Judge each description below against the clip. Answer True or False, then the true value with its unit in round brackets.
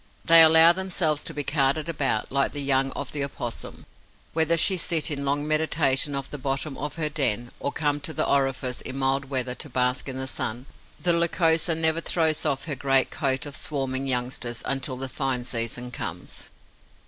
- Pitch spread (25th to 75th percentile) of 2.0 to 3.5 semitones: True (3.0 semitones)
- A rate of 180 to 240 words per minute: True (190 wpm)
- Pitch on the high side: False (140 Hz)